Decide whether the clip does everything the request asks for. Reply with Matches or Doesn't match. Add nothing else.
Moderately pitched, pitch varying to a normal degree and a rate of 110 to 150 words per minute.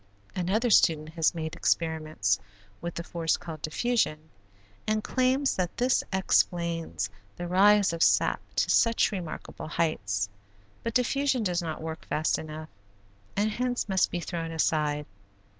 Matches